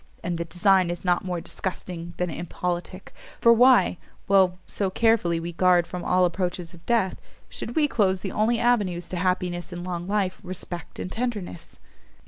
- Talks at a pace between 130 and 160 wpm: No, average, 170 wpm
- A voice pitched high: No, medium, 180 Hz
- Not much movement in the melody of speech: Yes, narrow, 2.2 semitones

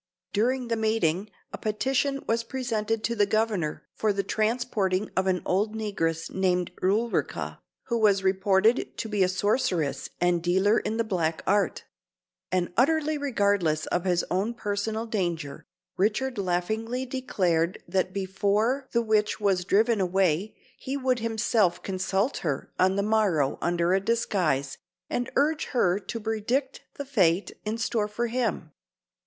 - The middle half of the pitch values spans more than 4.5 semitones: No, average, 3.8 semitones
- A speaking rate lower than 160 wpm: Yes, average, 150 wpm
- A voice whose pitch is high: Yes, high, 205 Hz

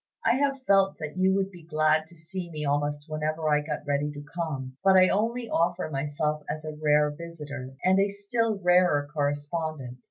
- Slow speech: No, average, 190 wpm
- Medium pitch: Yes, medium, 155 Hz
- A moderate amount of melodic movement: Yes, average, 4.1 semitones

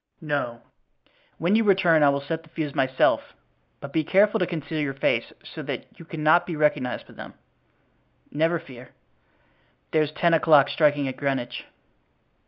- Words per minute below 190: Yes, average, 160 wpm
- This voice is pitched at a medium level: Yes, medium, 155 Hz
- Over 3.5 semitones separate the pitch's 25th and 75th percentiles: No, average, 3.0 semitones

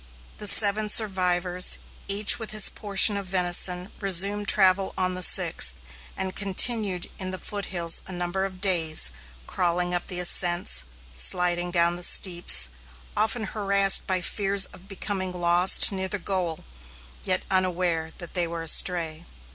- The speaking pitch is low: No, medium, 185 Hz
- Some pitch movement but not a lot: No, narrow, 2.1 semitones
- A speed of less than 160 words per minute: Yes, average, 145 wpm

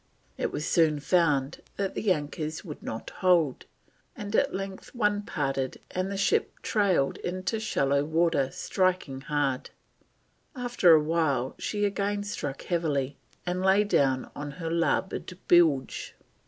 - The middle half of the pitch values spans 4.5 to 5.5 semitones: Yes, average, 5.2 semitones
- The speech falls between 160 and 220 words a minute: No, average, 140 wpm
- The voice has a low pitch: No, medium, 170 Hz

